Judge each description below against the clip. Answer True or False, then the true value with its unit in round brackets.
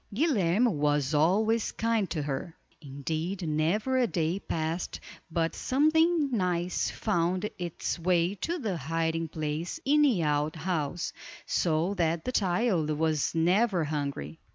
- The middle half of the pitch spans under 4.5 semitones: False (5.1 semitones)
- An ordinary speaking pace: False (130 wpm)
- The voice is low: False (170 Hz)